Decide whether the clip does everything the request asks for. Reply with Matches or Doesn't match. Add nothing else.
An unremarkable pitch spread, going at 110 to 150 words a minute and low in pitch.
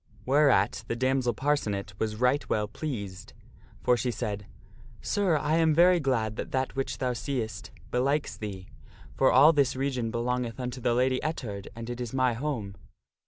Doesn't match